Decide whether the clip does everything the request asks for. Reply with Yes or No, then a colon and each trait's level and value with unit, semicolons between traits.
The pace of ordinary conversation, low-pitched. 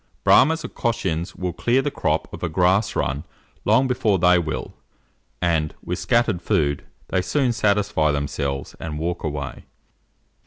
Yes: average, 150 wpm; very low, 90 Hz